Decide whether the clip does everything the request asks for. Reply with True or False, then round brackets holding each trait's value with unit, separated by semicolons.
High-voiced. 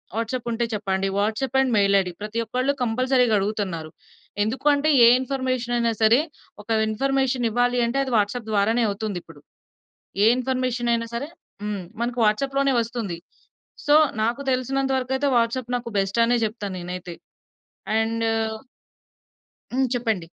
True (235 Hz)